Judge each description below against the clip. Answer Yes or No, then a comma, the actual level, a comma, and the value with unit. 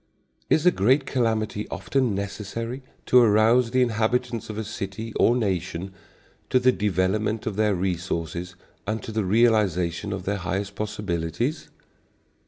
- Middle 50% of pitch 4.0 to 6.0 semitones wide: No, average, 3.3 semitones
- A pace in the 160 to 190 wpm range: No, average, 140 wpm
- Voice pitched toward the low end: Yes, low, 105 Hz